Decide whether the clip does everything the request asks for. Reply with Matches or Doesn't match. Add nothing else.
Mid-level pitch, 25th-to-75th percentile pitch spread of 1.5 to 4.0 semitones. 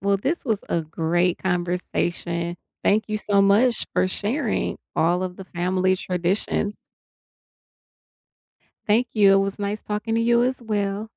Doesn't match